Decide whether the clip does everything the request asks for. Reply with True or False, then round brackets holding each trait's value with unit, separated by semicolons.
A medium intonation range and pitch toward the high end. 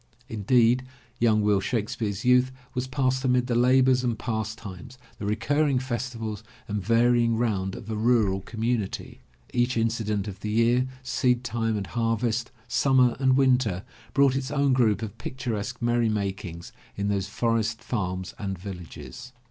False (3.1 semitones; 115 Hz)